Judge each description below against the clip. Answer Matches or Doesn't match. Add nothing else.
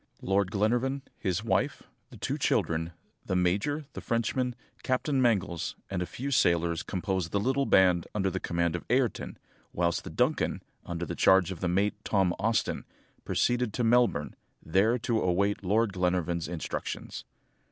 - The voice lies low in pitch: Matches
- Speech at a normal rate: Matches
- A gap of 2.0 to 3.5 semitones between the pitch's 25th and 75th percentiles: Doesn't match